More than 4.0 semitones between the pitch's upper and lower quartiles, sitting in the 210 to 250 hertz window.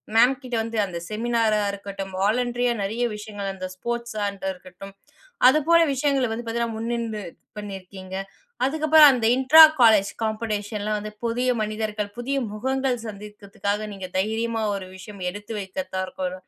No: average, 3.1 semitones; high, 215 Hz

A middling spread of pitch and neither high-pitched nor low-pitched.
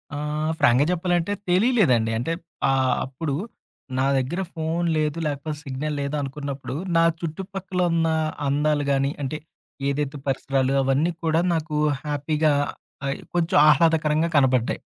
Yes: average, 3.2 semitones; medium, 150 Hz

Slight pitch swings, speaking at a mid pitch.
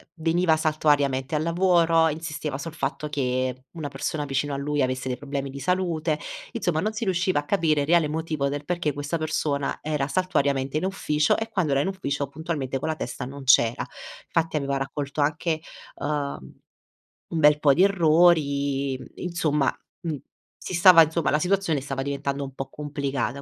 No: average, 3.0 semitones; medium, 150 Hz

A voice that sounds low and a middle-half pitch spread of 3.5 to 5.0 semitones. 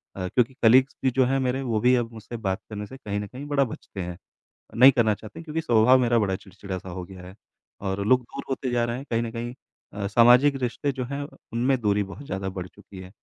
Yes: low, 115 Hz; average, 4.3 semitones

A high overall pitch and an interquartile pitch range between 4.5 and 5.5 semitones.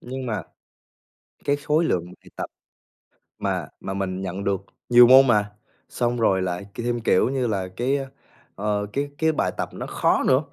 No: low, 115 Hz; average, 5.1 semitones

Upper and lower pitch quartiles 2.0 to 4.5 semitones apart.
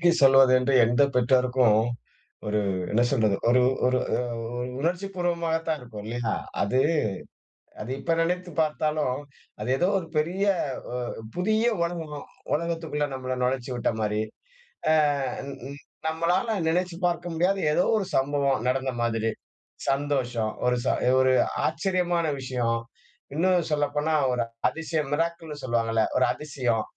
No: average, 5.3 semitones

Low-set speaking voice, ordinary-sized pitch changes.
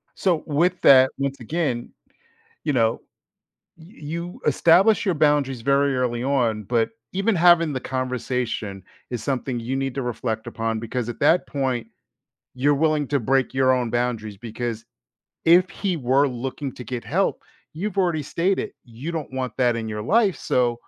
Yes: low, 130 Hz; average, 4.6 semitones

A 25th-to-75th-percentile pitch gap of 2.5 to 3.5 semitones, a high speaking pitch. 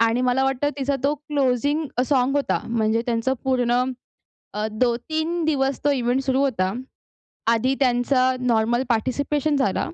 Yes: average, 2.8 semitones; very high, 255 Hz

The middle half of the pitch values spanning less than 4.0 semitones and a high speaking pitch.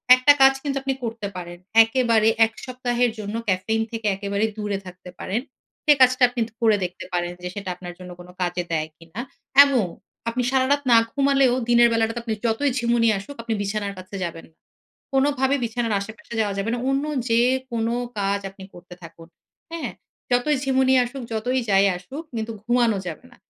No: average, 4.3 semitones; high, 225 Hz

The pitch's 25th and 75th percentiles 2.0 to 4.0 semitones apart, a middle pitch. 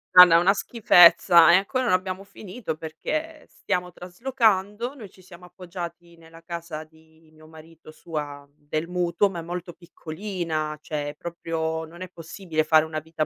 Yes: narrow, 2.6 semitones; medium, 170 Hz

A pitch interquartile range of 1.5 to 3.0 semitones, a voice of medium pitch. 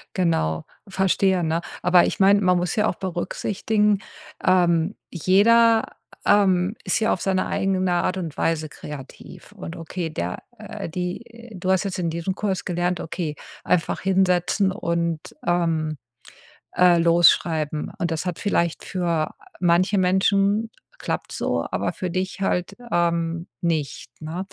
Yes: narrow, 2.4 semitones; medium, 180 Hz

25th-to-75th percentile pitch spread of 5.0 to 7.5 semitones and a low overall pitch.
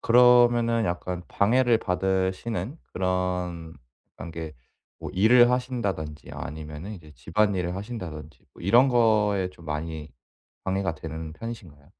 Yes: wide, 6.0 semitones; very low, 95 Hz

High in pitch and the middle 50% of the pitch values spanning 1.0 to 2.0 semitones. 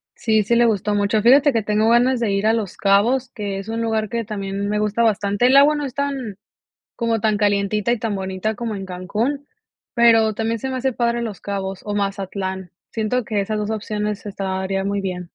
No: high, 215 Hz; average, 2.8 semitones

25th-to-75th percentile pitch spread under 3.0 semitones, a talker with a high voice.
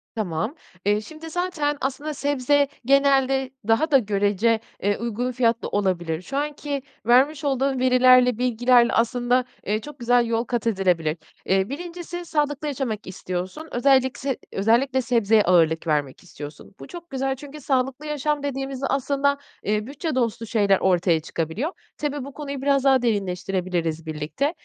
No: wide, 5.5 semitones; very high, 250 Hz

